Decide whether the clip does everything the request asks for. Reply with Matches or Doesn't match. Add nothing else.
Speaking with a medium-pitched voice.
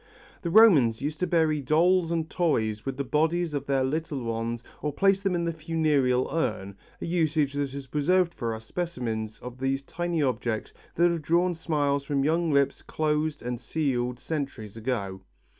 Matches